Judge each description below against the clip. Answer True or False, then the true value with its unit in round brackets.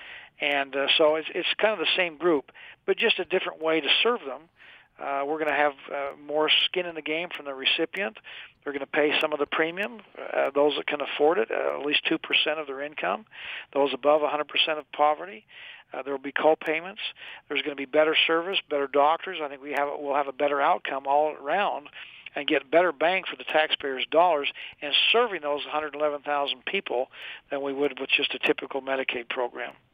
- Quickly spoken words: True (210 wpm)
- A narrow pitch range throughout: False (3.4 semitones)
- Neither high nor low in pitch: True (150 Hz)